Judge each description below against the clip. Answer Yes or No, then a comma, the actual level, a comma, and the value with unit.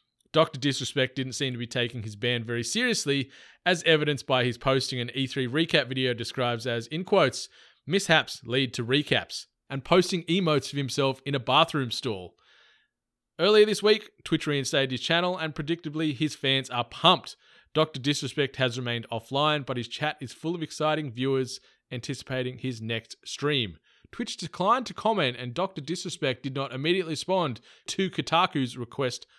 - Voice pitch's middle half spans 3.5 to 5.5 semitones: Yes, average, 3.9 semitones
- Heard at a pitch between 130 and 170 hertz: Yes, medium, 140 Hz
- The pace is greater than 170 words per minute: No, average, 165 wpm